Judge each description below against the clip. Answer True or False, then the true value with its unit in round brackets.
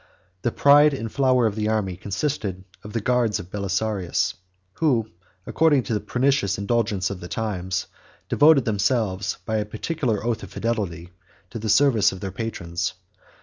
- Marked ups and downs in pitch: False (4.2 semitones)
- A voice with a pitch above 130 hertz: False (110 Hz)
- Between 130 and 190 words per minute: True (160 wpm)